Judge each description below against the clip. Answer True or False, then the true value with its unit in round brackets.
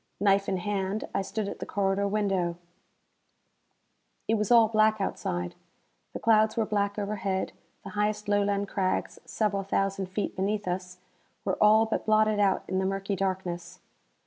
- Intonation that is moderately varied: False (1.9 semitones)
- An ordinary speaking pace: True (155 wpm)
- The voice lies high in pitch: True (200 Hz)